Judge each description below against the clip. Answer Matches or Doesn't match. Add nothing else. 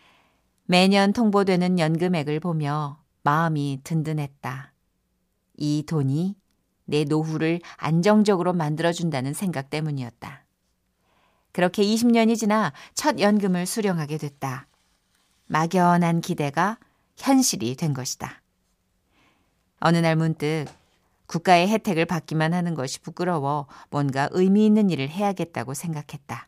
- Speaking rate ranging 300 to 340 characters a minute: Doesn't match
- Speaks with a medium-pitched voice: Matches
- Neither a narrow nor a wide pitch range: Matches